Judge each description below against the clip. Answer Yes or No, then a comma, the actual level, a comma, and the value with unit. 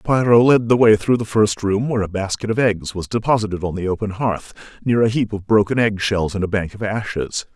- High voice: No, low, 105 Hz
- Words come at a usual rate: No, fast, 245 wpm